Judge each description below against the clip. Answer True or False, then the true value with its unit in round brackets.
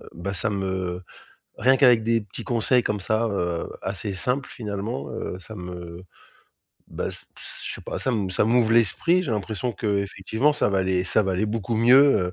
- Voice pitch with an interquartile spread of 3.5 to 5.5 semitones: True (3.8 semitones)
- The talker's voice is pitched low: True (105 Hz)